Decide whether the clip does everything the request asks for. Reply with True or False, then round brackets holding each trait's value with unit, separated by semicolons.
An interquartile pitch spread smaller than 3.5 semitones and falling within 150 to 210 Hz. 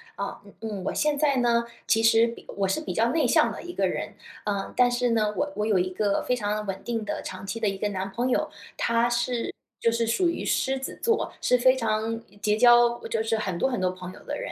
False (3.0 semitones; 230 Hz)